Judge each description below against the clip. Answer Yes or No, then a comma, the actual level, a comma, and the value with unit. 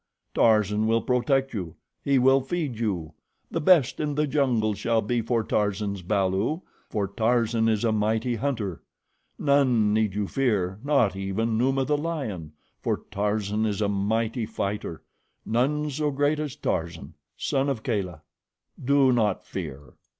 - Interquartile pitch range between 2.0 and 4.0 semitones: No, average, 4.7 semitones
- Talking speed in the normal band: Yes, average, 150 wpm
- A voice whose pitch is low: Yes, low, 115 Hz